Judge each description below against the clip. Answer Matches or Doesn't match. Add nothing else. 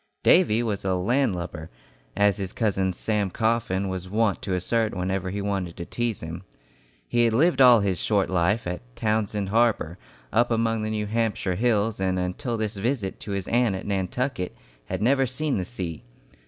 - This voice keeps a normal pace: Matches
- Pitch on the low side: Matches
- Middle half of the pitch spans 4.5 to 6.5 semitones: Doesn't match